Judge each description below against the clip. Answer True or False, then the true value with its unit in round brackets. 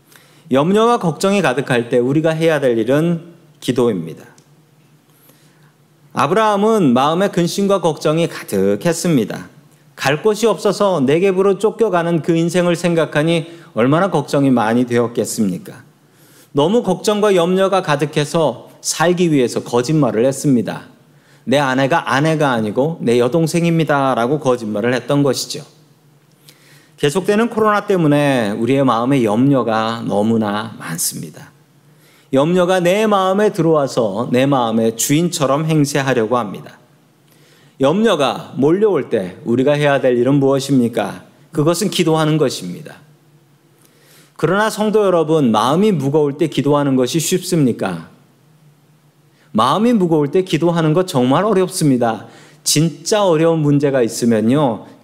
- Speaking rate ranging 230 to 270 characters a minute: False (295 characters per minute)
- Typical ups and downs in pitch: True (3.7 semitones)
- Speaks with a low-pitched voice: False (155 Hz)